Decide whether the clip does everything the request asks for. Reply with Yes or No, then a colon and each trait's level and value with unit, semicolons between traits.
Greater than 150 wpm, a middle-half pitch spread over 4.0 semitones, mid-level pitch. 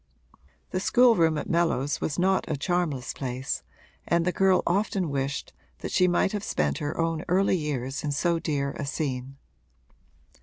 Yes: average, 160 wpm; average, 4.5 semitones; medium, 160 Hz